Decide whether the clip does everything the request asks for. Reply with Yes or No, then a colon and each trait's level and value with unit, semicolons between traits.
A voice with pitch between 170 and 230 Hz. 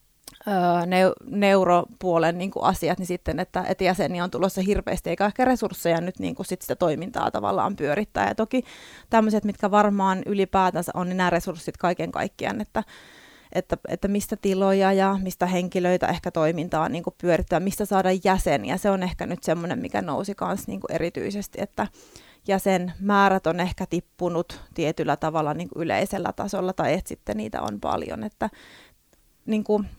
Yes: medium, 185 Hz